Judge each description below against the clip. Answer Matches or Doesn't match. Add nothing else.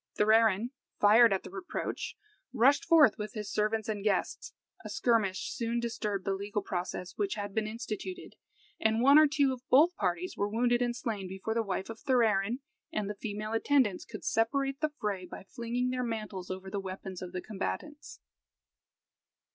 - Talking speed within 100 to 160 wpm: Doesn't match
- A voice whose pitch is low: Doesn't match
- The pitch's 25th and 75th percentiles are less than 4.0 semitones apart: Matches